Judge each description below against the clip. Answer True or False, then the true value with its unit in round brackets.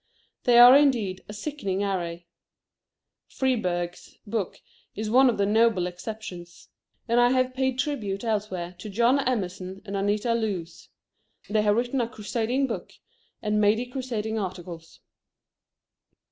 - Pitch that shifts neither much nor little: True (4.2 semitones)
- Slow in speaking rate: True (130 wpm)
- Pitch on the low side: False (215 Hz)